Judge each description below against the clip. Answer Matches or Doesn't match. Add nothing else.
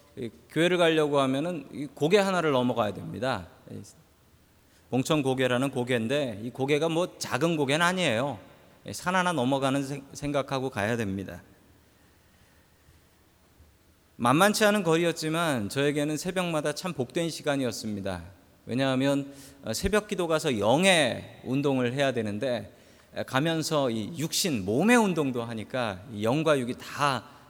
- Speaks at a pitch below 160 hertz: Matches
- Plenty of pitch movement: Matches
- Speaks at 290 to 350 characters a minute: Doesn't match